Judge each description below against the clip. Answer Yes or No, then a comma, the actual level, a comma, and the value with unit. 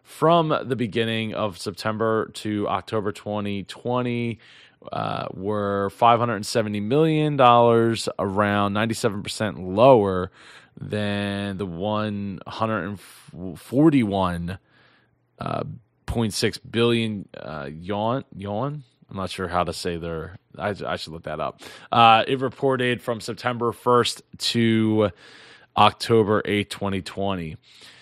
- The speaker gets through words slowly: Yes, slow, 95 wpm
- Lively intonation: No, average, 3.0 semitones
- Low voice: Yes, low, 105 Hz